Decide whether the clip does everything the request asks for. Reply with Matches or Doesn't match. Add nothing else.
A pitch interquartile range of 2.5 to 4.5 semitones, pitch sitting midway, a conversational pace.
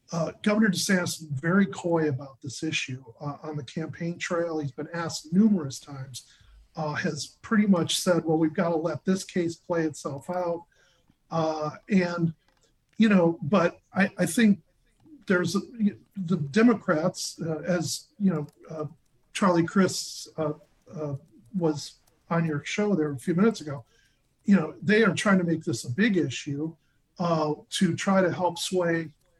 Matches